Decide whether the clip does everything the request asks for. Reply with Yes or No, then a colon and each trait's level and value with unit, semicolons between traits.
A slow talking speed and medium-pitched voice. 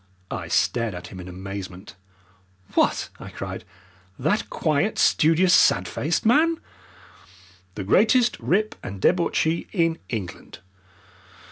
Yes: slow, 115 wpm; medium, 160 Hz